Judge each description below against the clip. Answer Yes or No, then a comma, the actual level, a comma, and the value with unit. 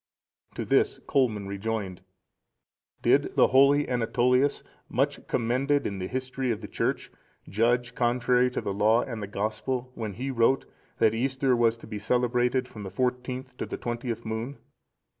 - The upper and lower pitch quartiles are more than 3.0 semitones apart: No, narrow, 2.6 semitones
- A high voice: No, low, 120 Hz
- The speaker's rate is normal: Yes, average, 160 wpm